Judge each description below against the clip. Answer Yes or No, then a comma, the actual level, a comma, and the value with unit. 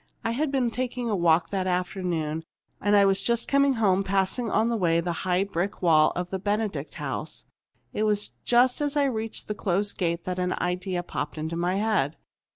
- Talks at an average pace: Yes, average, 195 wpm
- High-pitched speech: Yes, high, 195 Hz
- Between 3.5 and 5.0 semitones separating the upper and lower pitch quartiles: Yes, average, 4.1 semitones